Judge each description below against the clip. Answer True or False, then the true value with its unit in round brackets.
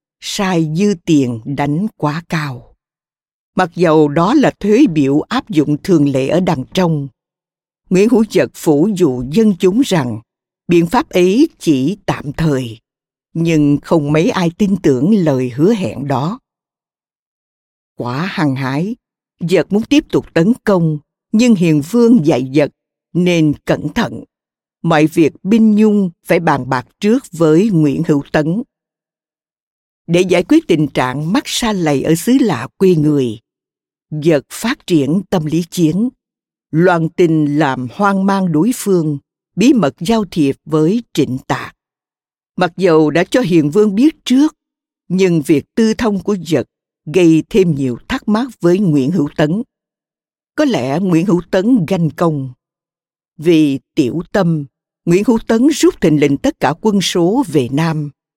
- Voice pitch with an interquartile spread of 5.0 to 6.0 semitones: True (5.3 semitones)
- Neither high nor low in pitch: True (170 Hz)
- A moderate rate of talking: False (155 wpm)